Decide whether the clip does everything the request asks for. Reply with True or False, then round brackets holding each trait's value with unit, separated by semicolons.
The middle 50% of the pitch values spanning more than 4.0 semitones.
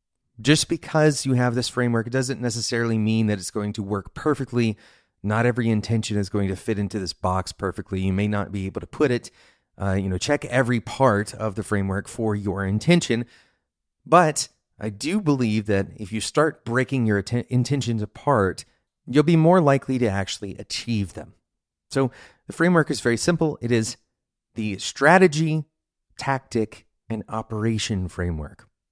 True (4.6 semitones)